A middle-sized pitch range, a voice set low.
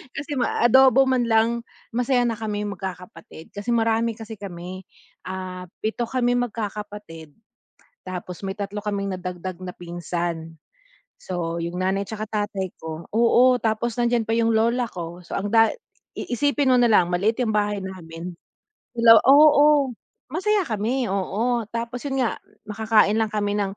No: average, 4.3 semitones; high, 215 Hz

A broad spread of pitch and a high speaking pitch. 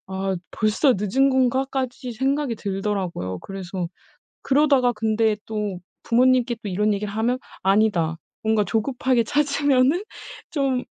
No: average, 4.5 semitones; high, 225 Hz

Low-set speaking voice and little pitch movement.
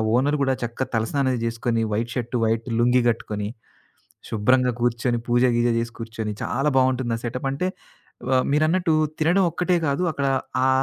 No: low, 125 Hz; average, 3.0 semitones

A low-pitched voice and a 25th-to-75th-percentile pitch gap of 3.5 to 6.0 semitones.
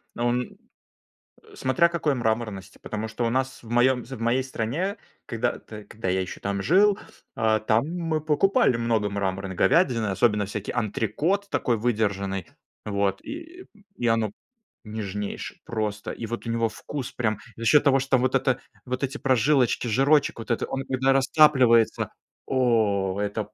Yes: low, 120 Hz; average, 4.1 semitones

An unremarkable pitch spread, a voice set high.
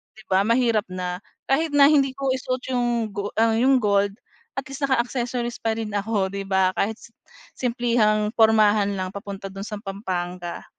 Yes: average, 3.7 semitones; high, 220 Hz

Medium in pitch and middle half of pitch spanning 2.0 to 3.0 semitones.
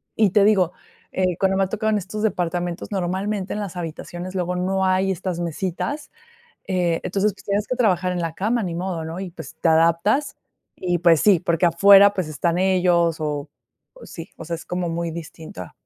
Yes: medium, 180 Hz; narrow, 2.5 semitones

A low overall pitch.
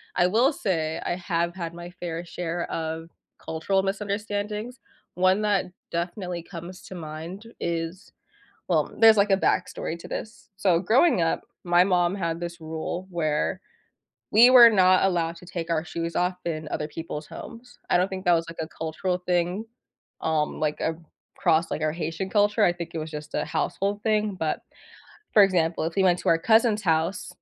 No: medium, 175 Hz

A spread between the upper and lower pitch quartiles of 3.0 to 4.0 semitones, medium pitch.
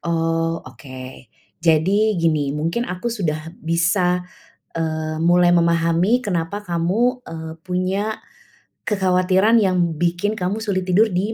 Yes: average, 3.4 semitones; medium, 175 Hz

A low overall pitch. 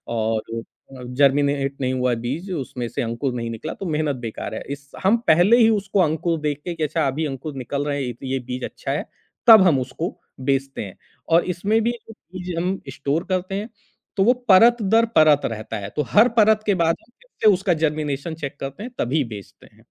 No: medium, 150 Hz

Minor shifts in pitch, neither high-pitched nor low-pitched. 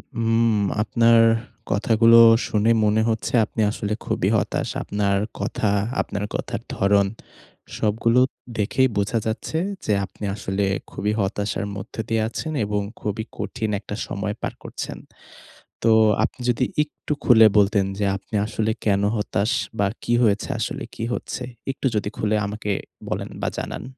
No: narrow, 1.9 semitones; low, 105 Hz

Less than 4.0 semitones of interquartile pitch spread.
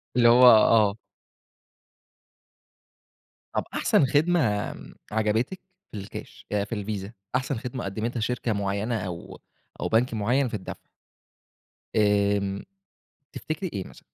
Yes: average, 3.5 semitones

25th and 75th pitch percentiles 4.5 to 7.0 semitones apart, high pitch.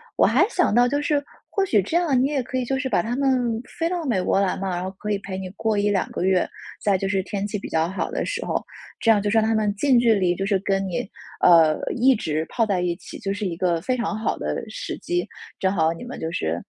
Yes: average, 5.2 semitones; high, 210 Hz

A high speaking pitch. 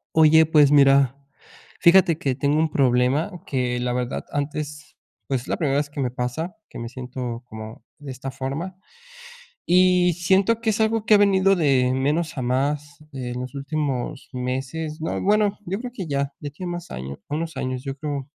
No: medium, 145 Hz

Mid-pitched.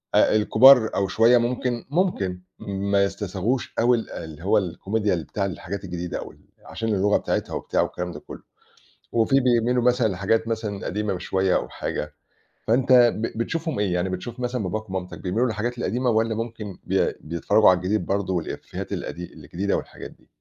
No: low, 105 Hz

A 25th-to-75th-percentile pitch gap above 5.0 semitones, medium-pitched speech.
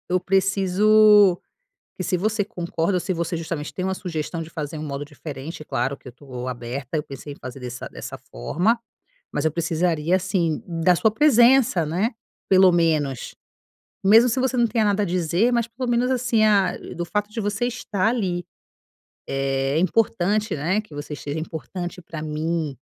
Yes: wide, 5.4 semitones; medium, 175 Hz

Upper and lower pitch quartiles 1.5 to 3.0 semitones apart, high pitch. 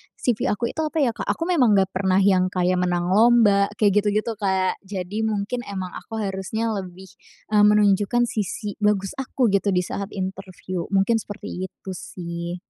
Yes: narrow, 2.5 semitones; high, 200 Hz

